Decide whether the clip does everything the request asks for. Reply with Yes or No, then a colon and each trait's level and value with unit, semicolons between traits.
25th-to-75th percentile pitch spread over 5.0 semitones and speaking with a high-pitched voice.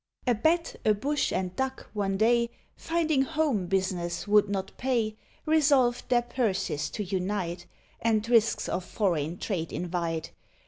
Yes: wide, 5.5 semitones; high, 215 Hz